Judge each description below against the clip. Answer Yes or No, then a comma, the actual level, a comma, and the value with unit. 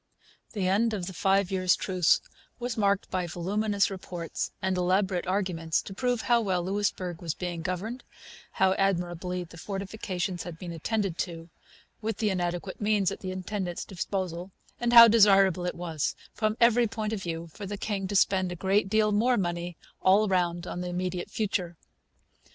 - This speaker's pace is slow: No, average, 175 wpm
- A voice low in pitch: No, high, 190 Hz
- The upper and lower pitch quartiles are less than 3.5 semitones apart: Yes, average, 2.7 semitones